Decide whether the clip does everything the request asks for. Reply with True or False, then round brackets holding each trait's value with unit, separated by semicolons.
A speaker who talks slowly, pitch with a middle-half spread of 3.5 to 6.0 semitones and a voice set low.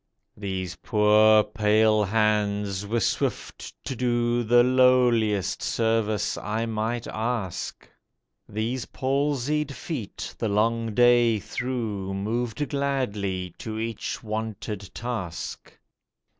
False (100 wpm; 2.6 semitones; 110 Hz)